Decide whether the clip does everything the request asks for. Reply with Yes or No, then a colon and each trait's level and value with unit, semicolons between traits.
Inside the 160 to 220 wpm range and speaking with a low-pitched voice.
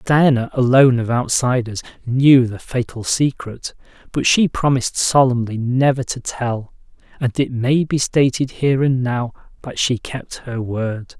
No: average, 150 wpm; low, 125 Hz